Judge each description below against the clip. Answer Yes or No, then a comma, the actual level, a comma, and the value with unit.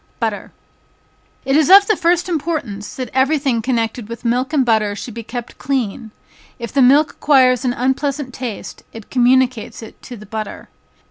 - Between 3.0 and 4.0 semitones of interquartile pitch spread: Yes, average, 3.4 semitones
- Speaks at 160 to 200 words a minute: Yes, average, 175 wpm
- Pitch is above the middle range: Yes, very high, 255 Hz